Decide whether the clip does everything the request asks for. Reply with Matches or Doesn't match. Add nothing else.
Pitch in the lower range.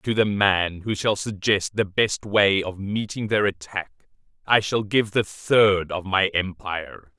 Matches